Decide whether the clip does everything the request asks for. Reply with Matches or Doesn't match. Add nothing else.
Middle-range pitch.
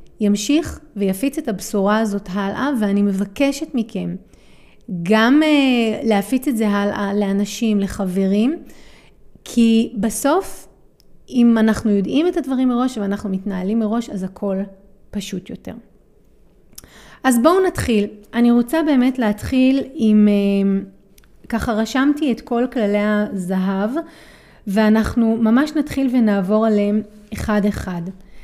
Doesn't match